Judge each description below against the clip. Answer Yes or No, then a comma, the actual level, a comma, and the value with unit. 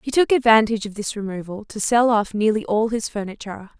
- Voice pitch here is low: No, high, 215 Hz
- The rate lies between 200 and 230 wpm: Yes, fast, 205 wpm